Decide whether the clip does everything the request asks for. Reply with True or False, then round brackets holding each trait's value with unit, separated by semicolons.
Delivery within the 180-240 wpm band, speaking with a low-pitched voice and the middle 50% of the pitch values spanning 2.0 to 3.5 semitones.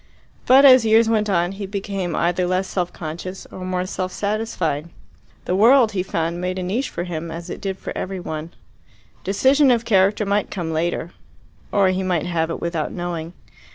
False (190 wpm; 185 Hz; 3.1 semitones)